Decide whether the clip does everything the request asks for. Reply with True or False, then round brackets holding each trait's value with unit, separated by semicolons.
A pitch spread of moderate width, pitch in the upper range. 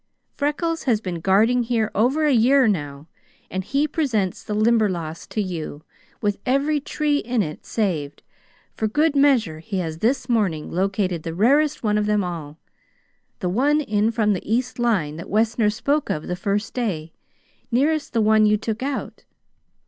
False (5.7 semitones; 215 Hz)